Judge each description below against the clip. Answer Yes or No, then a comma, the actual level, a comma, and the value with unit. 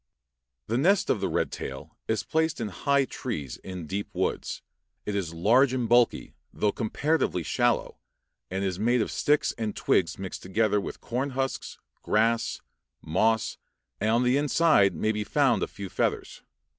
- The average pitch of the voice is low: Yes, low, 110 Hz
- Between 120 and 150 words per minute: No, average, 165 wpm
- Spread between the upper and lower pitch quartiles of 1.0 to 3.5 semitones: No, average, 4.9 semitones